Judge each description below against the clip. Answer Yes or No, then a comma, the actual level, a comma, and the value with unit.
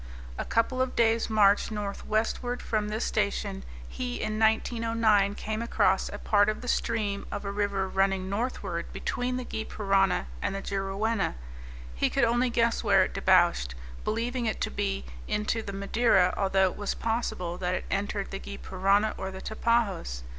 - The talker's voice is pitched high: Yes, high, 210 Hz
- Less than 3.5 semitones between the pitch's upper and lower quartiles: Yes, average, 2.8 semitones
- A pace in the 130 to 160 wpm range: No, average, 170 wpm